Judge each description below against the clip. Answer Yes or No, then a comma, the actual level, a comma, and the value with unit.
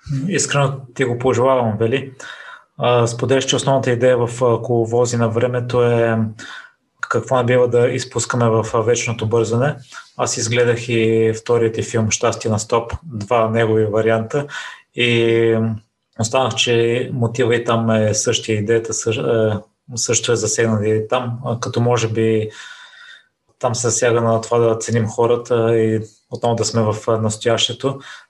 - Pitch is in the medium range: No, low, 115 Hz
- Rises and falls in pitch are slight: Yes, narrow, 1.7 semitones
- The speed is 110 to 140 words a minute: Yes, average, 135 wpm